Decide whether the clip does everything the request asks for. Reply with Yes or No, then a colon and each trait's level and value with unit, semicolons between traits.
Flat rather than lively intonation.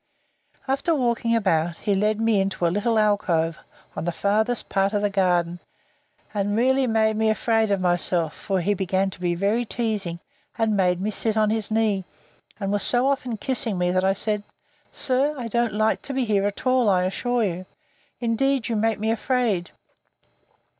No: average, 3.3 semitones